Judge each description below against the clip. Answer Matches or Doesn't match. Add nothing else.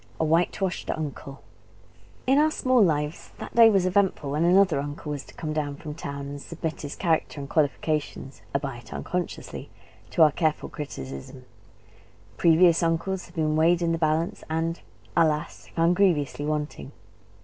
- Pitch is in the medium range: Matches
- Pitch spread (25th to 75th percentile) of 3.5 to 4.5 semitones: Doesn't match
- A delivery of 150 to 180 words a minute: Matches